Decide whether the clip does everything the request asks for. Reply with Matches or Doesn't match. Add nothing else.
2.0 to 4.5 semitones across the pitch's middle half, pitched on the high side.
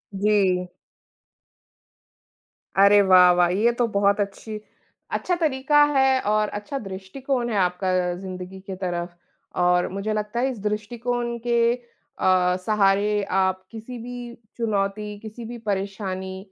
Matches